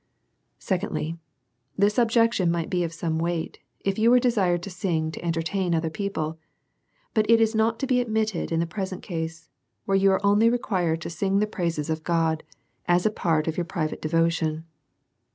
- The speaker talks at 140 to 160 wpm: No, average, 185 wpm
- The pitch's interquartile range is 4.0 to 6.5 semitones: Yes, average, 4.3 semitones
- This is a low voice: No, medium, 175 Hz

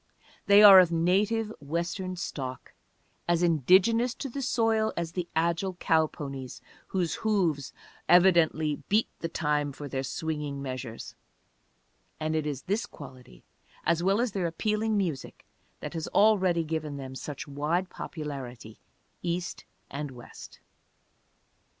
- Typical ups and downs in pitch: Yes, average, 4.8 semitones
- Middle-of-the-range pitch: Yes, medium, 165 Hz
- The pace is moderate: No, slow, 130 wpm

